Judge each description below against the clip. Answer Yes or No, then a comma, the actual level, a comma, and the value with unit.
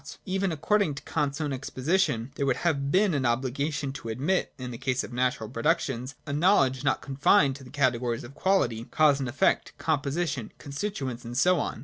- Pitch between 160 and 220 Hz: No, medium, 140 Hz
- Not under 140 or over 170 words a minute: No, average, 190 wpm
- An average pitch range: Yes, average, 3.7 semitones